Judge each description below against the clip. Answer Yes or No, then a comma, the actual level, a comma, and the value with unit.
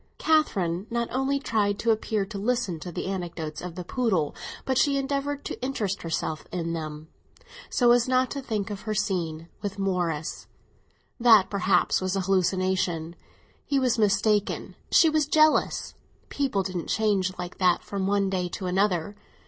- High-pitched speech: Yes, high, 195 Hz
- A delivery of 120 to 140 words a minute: No, average, 165 wpm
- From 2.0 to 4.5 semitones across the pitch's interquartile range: No, average, 4.9 semitones